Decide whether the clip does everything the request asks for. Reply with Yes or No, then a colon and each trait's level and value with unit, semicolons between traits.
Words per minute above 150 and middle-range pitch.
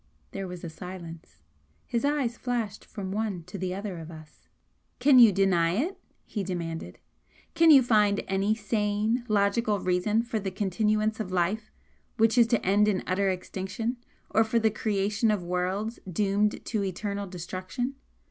No: average, 160 wpm; high, 205 Hz